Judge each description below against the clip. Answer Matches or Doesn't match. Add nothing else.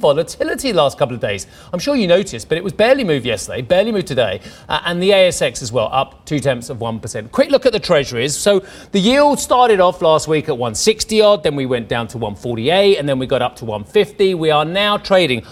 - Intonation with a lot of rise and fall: Matches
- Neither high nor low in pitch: Matches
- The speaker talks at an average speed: Doesn't match